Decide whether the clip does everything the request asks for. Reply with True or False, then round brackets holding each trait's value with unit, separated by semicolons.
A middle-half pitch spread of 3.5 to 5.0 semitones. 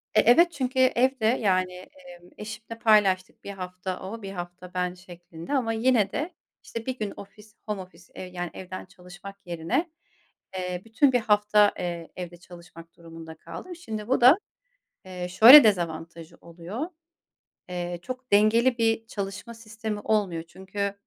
True (4.3 semitones)